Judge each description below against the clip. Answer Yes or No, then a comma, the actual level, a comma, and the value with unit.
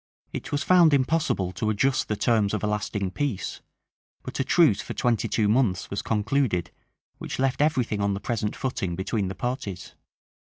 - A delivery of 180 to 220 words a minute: Yes, average, 185 wpm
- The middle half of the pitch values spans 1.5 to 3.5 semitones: No, average, 4.9 semitones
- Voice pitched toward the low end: Yes, low, 110 Hz